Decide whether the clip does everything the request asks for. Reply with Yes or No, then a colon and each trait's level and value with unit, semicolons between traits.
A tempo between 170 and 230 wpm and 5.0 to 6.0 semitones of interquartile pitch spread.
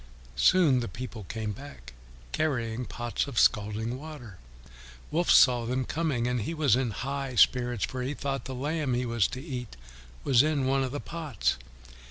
No: average, 180 wpm; average, 3.2 semitones